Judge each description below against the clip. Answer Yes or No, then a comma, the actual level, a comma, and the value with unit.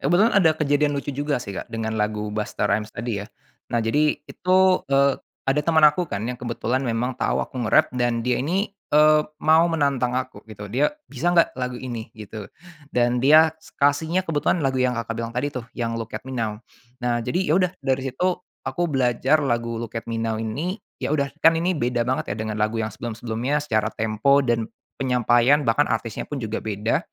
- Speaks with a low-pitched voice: Yes, low, 125 Hz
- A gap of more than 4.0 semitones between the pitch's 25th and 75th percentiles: Yes, average, 4.4 semitones